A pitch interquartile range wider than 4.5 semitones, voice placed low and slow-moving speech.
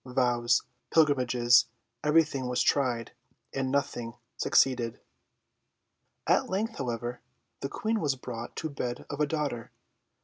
No: average, 3.4 semitones; low, 130 Hz; slow, 115 wpm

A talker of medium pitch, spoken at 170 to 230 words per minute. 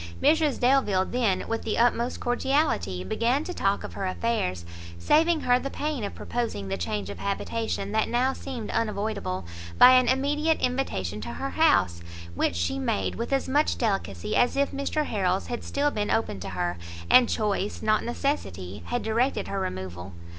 No: high, 220 Hz; average, 175 wpm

